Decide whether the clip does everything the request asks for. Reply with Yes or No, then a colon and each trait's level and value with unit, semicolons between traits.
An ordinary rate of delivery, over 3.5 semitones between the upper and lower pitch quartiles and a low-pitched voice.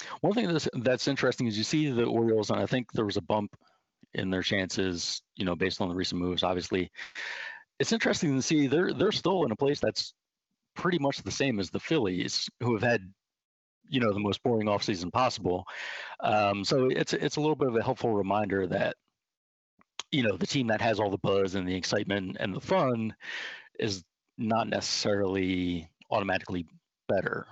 Yes: average, 190 wpm; average, 5.2 semitones; low, 105 Hz